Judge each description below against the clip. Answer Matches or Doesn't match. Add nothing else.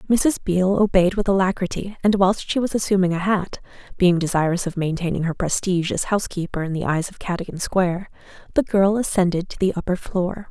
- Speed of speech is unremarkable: Matches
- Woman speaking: Matches